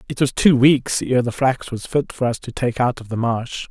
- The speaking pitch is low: Yes, low, 125 Hz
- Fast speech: Yes, fast, 275 wpm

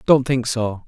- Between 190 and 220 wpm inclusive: Yes, fast, 205 wpm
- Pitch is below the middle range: Yes, low, 120 Hz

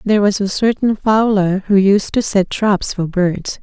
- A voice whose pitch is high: Yes, high, 200 Hz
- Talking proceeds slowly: No, average, 200 wpm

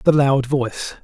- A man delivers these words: Yes, male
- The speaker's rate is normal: Yes, average, 175 wpm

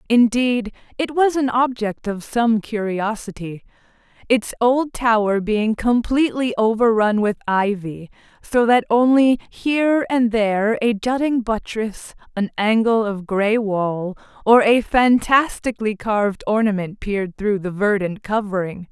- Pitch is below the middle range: No, high, 220 Hz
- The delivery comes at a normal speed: No, slow, 125 wpm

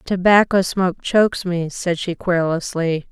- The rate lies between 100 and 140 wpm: Yes, slow, 135 wpm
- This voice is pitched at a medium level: Yes, medium, 180 Hz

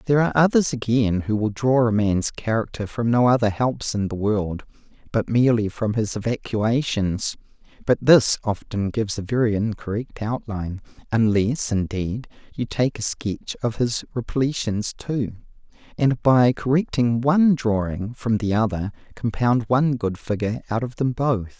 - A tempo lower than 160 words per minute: Yes, average, 150 wpm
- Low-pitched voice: Yes, low, 115 Hz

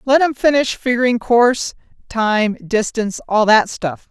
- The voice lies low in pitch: No, high, 230 Hz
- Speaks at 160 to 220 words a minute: No, average, 145 wpm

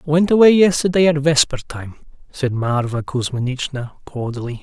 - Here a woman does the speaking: No, male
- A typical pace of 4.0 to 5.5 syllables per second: Yes, 5.2 syllables/s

